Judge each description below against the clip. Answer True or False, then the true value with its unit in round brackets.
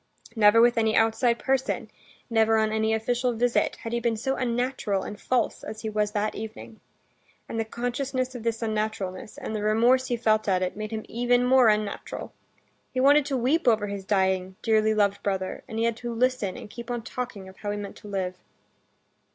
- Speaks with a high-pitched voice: True (225 Hz)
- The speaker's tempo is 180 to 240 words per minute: True (200 wpm)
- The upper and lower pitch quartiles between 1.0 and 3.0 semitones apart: True (2.6 semitones)